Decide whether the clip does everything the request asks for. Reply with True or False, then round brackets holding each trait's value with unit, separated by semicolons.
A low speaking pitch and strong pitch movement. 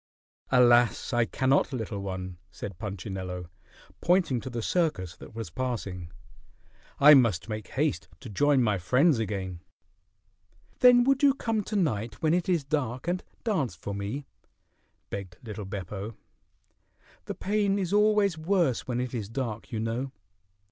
True (120 Hz; 7.9 semitones)